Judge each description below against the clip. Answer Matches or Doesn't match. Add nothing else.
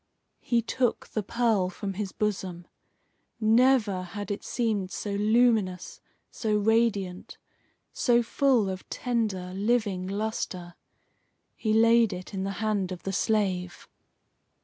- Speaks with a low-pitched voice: Doesn't match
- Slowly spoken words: Matches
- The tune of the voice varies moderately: Matches